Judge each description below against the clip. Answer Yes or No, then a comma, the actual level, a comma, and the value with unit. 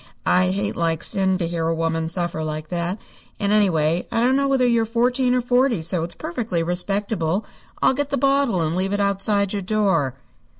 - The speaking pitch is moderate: No, high, 195 Hz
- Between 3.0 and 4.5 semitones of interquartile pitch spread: No, wide, 5.6 semitones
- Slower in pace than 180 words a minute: No, average, 200 wpm